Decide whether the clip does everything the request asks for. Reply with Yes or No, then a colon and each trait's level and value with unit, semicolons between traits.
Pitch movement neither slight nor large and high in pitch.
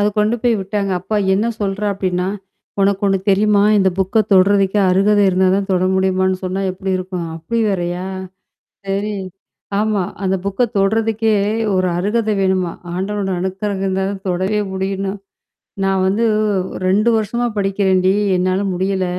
No: narrow, 1.7 semitones; high, 195 Hz